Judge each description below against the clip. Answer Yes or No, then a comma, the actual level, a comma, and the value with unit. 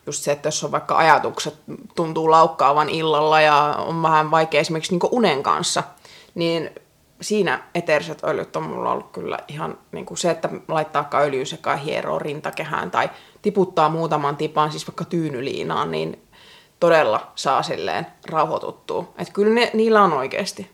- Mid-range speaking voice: Yes, medium, 160 Hz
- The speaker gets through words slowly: No, fast, 155 wpm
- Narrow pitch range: No, average, 3.7 semitones